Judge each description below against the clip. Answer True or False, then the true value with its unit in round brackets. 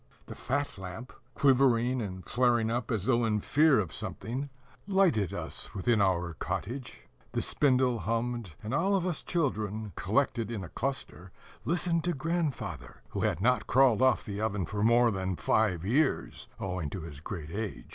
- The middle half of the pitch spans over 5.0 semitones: True (5.5 semitones)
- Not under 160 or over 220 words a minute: True (165 wpm)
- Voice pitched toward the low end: True (115 Hz)